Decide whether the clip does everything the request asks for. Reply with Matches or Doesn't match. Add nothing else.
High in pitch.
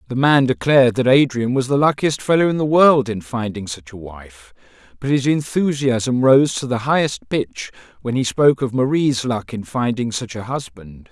Doesn't match